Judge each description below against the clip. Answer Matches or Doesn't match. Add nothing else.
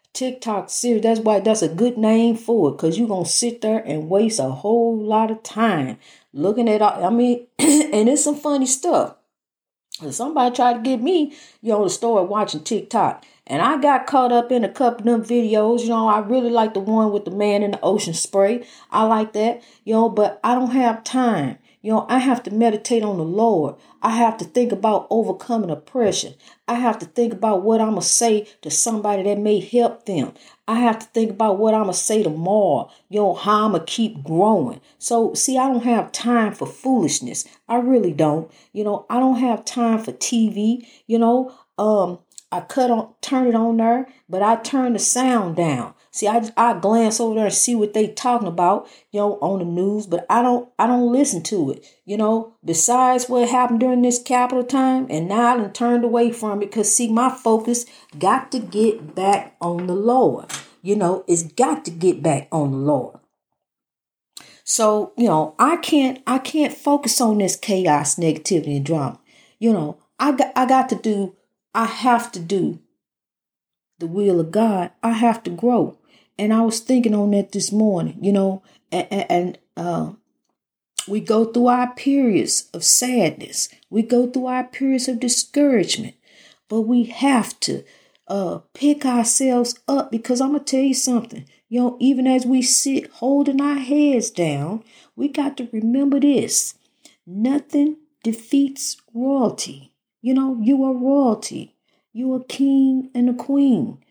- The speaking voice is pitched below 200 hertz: Doesn't match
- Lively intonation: Doesn't match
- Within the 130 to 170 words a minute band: Doesn't match